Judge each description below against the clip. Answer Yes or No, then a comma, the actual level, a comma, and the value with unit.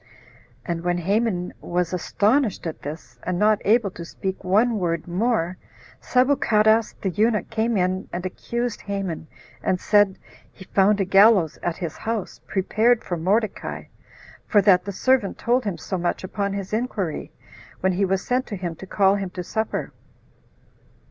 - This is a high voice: Yes, high, 195 Hz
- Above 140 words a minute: Yes, average, 160 wpm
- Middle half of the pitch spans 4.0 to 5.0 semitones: No, average, 3.4 semitones